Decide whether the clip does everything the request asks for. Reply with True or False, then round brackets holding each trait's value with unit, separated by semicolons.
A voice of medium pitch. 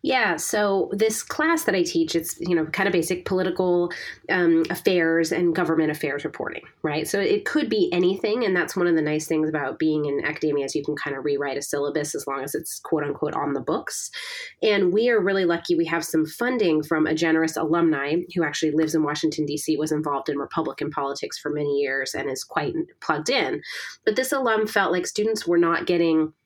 True (165 Hz)